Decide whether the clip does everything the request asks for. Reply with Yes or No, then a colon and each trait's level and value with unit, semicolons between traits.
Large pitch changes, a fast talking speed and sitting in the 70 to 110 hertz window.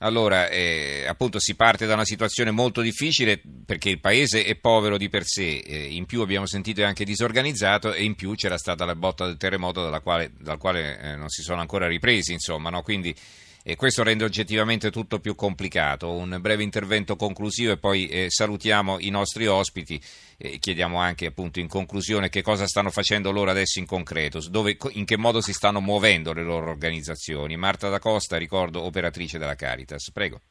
No: average, 3.7 semitones; fast, 190 wpm; low, 100 Hz